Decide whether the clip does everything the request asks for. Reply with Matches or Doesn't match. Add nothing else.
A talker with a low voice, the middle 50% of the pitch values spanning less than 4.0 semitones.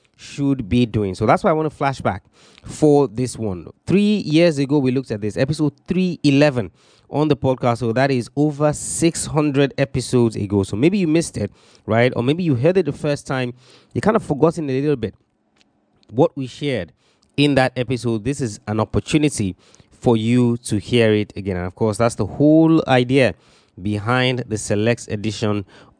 Doesn't match